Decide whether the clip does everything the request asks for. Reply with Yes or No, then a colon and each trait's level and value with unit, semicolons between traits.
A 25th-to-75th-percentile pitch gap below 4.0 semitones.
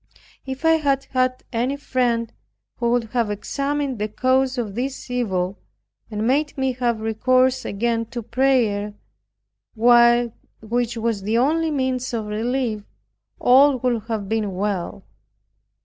Yes: average, 3.0 semitones